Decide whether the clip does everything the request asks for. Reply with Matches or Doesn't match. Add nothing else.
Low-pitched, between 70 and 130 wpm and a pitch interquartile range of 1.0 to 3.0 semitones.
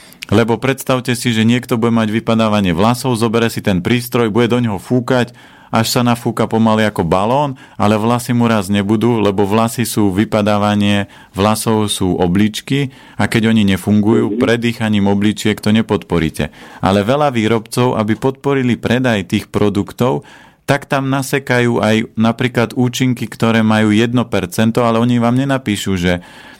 Doesn't match